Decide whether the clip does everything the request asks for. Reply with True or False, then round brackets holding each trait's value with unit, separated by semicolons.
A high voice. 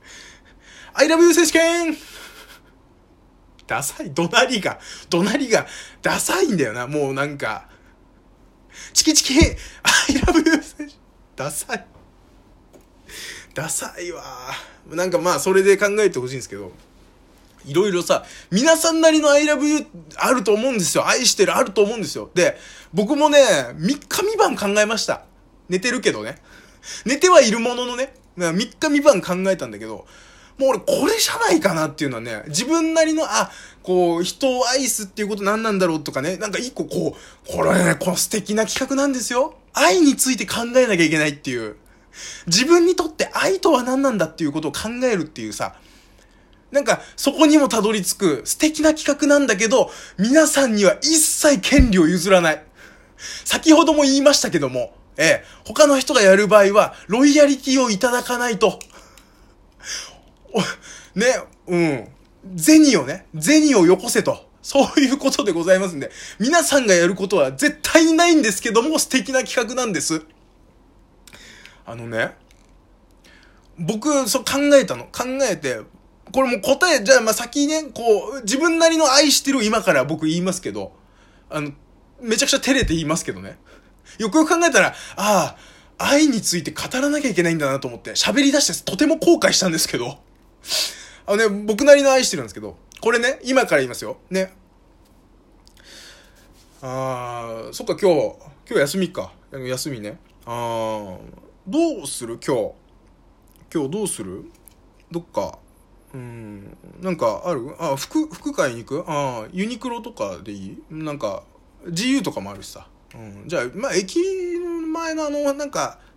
True (225 Hz)